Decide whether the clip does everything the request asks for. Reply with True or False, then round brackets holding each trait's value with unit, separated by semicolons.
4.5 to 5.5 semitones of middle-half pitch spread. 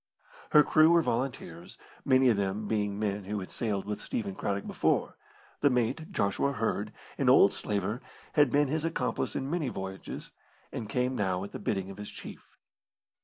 True (5.2 semitones)